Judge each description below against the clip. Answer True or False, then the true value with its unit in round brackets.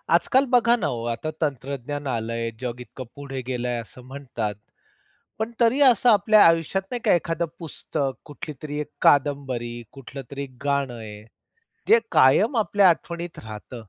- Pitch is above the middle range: False (140 Hz)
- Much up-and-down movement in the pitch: True (5.8 semitones)